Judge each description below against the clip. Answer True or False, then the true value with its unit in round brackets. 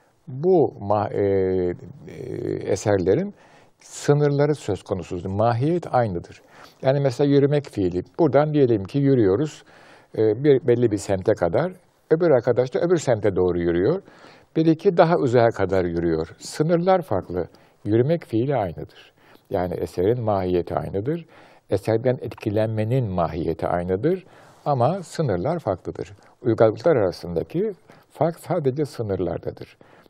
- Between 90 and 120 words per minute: True (110 wpm)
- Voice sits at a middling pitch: False (125 Hz)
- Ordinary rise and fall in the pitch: False (7.2 semitones)